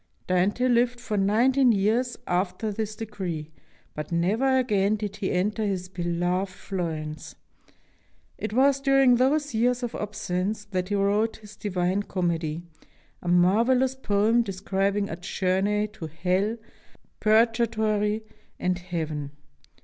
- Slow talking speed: Yes, slow, 125 wpm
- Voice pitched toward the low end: No, high, 205 Hz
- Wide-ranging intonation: No, average, 3.8 semitones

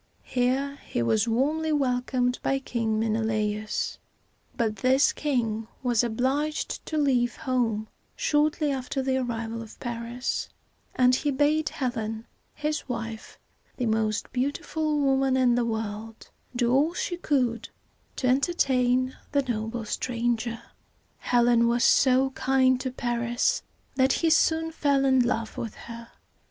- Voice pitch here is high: Yes, very high, 250 Hz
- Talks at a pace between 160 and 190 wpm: No, slow, 135 wpm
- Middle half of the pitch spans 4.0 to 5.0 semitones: No, average, 2.9 semitones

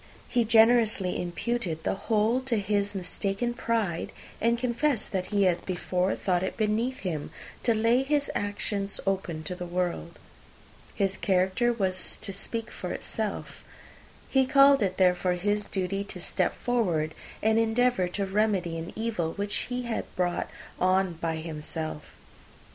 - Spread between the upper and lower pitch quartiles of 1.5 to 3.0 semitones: No, average, 4.3 semitones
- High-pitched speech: Yes, high, 200 Hz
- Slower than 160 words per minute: Yes, average, 150 wpm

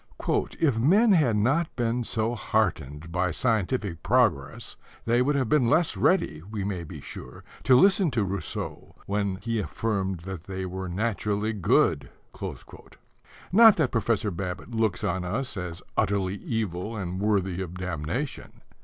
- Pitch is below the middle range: Yes, low, 105 Hz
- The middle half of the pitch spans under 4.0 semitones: No, average, 4.6 semitones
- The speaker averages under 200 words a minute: Yes, average, 145 wpm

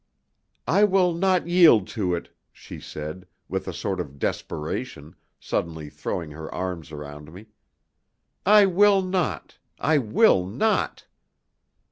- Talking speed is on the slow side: Yes, slow, 125 wpm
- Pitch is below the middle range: Yes, low, 100 Hz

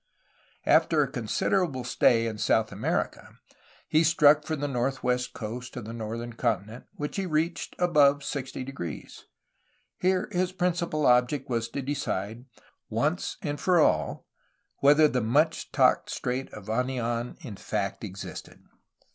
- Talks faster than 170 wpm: No, slow, 135 wpm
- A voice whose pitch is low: Yes, low, 130 Hz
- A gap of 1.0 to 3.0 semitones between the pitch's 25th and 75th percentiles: No, average, 4.8 semitones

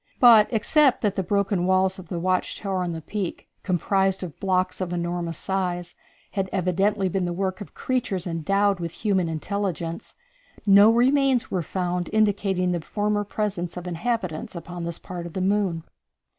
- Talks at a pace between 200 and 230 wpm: No, average, 170 wpm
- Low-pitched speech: No, medium, 185 Hz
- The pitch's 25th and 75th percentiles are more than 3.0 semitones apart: No, narrow, 2.6 semitones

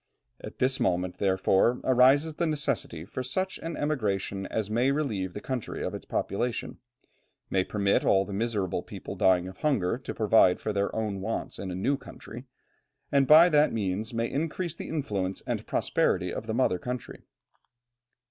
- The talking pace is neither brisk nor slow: Yes, average, 170 wpm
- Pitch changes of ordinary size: No, wide, 6.1 semitones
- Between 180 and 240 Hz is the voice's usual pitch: No, low, 115 Hz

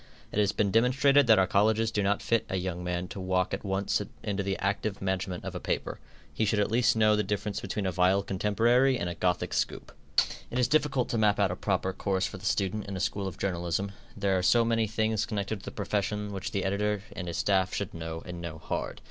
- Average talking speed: No, fast, 240 wpm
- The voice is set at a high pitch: No, low, 100 Hz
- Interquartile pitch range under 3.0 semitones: Yes, narrow, 2.5 semitones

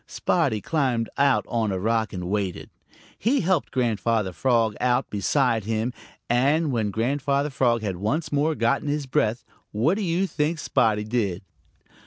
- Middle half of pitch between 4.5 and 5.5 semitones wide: Yes, average, 4.9 semitones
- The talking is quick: No, average, 155 wpm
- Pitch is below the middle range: Yes, low, 120 Hz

